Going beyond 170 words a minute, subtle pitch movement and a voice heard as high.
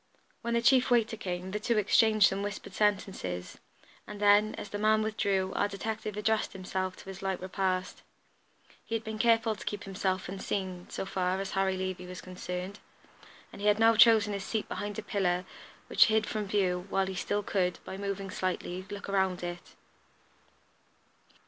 Yes: average, 180 wpm; narrow, 2.2 semitones; high, 195 Hz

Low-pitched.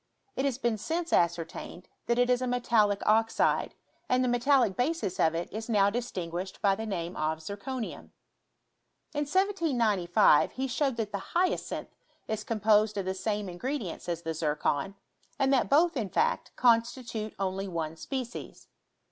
No: high, 220 Hz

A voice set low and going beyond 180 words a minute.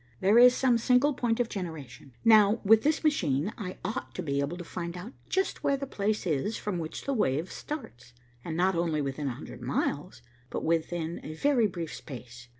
No: medium, 180 Hz; average, 200 wpm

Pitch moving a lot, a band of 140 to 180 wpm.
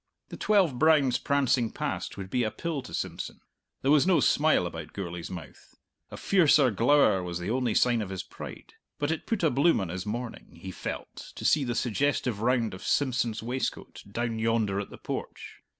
No: wide, 6.1 semitones; average, 195 wpm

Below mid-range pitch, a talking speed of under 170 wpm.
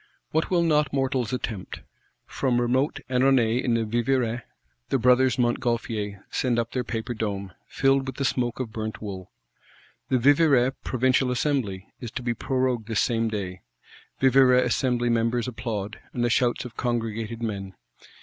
Yes: low, 120 Hz; average, 155 wpm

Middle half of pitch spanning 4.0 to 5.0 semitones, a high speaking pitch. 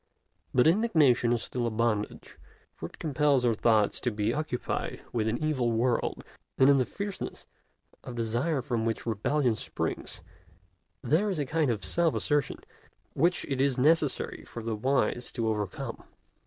No: average, 4.5 semitones; low, 125 Hz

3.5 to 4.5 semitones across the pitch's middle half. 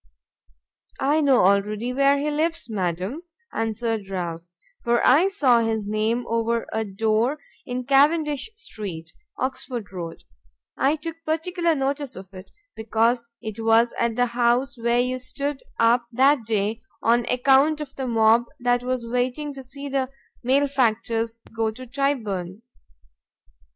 Yes: average, 3.8 semitones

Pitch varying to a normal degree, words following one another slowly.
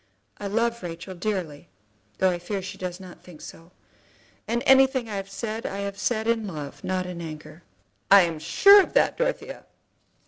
No: average, 4.5 semitones; average, 175 wpm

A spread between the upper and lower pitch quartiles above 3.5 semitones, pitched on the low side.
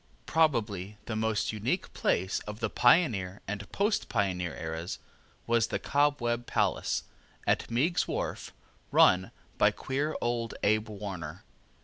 Yes: average, 4.2 semitones; low, 110 Hz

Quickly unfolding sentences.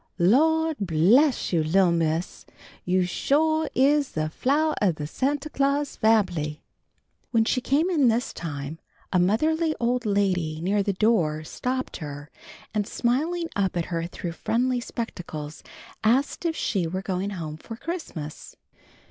No: average, 145 wpm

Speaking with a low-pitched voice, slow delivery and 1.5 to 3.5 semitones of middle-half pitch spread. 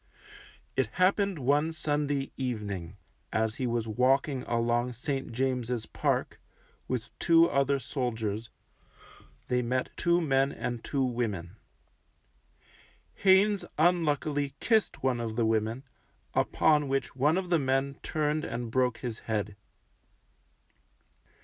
No: low, 130 Hz; slow, 120 wpm; average, 4.1 semitones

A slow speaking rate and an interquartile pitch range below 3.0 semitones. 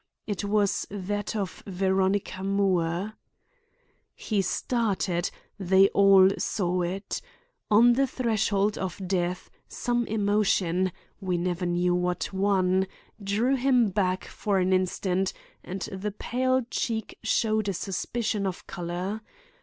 Yes: slow, 115 wpm; narrow, 2.5 semitones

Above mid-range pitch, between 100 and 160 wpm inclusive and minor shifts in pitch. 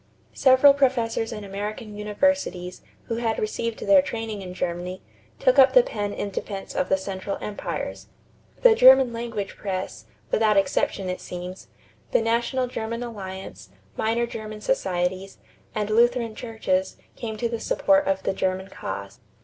No: high, 215 Hz; average, 150 wpm; average, 3.8 semitones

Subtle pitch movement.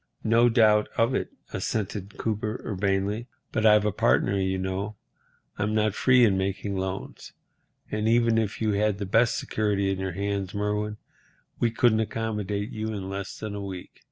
Yes: narrow, 2.0 semitones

